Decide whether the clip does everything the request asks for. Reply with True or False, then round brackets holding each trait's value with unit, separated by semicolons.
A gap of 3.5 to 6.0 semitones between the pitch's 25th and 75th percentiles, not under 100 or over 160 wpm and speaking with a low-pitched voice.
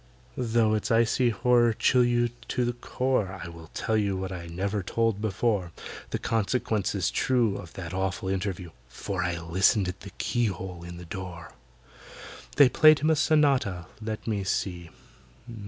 True (4.5 semitones; 155 wpm; 100 Hz)